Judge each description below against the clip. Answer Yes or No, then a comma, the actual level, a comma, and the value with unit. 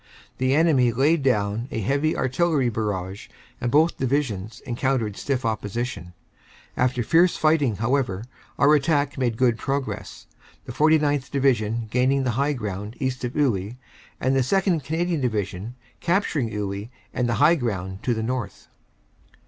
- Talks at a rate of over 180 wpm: No, average, 145 wpm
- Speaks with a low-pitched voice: Yes, low, 125 Hz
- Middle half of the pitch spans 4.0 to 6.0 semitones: Yes, average, 4.4 semitones